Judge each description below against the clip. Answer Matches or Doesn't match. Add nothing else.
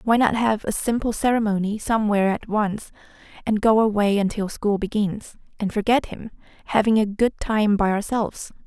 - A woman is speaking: Matches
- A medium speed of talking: Matches